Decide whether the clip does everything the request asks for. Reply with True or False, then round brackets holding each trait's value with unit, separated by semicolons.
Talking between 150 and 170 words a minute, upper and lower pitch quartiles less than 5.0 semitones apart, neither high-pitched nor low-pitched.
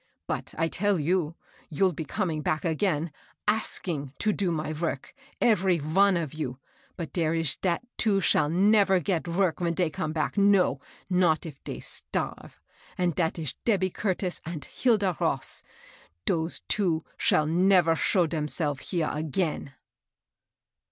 True (160 wpm; 3.5 semitones; 170 Hz)